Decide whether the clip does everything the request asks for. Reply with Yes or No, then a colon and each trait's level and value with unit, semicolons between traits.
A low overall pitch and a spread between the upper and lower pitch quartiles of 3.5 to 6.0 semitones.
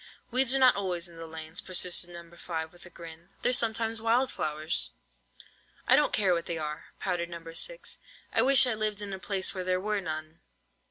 No: medium, 180 Hz; average, 4.6 semitones